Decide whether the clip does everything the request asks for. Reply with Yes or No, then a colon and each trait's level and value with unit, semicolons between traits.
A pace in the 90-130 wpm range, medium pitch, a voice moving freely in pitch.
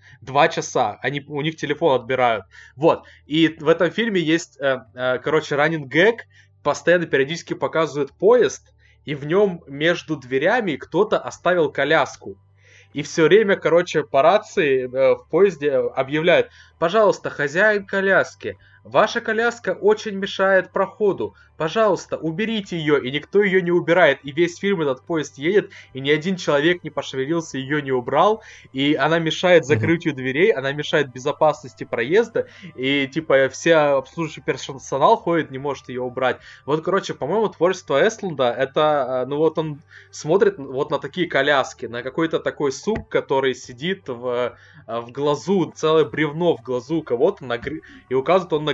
No: average, 145 wpm; medium, 155 Hz; wide, 6.0 semitones